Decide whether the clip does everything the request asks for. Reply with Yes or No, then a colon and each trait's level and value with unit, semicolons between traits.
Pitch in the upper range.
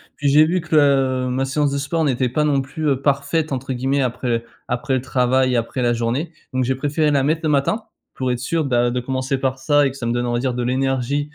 No: low, 135 Hz